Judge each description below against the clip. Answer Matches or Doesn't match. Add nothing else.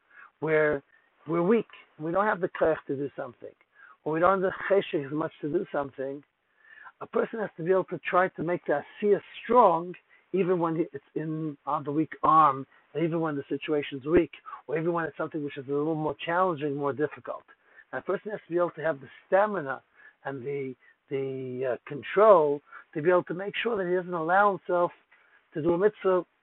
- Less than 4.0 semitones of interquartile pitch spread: Doesn't match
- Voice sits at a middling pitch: Matches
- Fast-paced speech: Matches